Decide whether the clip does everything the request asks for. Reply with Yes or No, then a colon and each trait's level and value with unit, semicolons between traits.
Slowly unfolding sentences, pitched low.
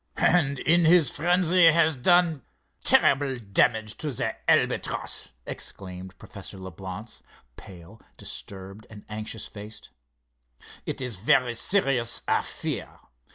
Yes: slow, 110 wpm; low, 120 Hz